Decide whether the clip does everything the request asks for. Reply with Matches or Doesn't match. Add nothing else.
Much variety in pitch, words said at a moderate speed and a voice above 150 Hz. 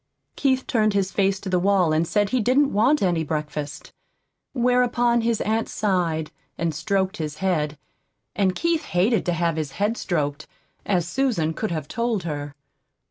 Matches